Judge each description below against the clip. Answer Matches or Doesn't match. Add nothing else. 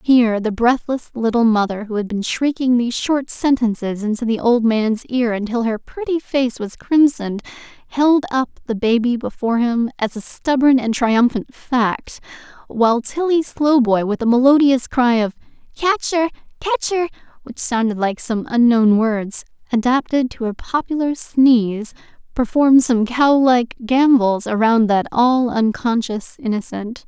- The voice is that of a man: Doesn't match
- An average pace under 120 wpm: Doesn't match